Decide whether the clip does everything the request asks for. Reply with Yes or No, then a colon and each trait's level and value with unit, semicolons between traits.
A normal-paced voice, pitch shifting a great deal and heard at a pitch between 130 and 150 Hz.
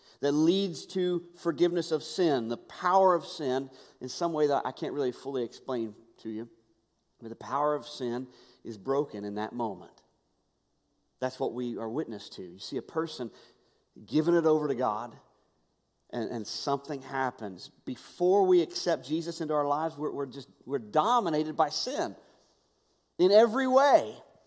Yes: average, 170 wpm; wide, 6.4 semitones; medium, 140 Hz